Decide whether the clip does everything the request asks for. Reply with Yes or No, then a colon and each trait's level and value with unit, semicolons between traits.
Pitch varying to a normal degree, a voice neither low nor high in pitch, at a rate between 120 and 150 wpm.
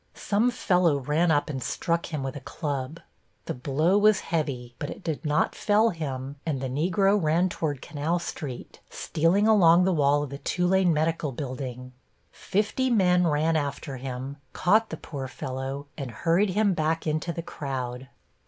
No: average, 4.6 semitones; medium, 155 Hz; average, 170 wpm